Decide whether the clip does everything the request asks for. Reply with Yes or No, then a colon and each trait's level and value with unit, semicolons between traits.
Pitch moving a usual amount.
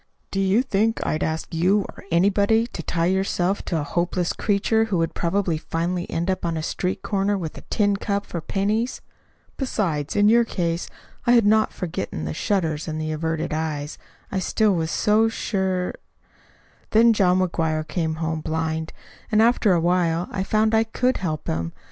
Yes: average, 4.1 semitones